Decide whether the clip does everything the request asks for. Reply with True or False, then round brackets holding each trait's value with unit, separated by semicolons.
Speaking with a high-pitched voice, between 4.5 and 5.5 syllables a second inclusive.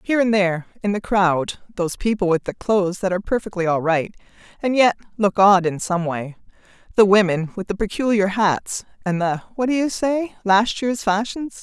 True (200 Hz; 5.3 syllables/s)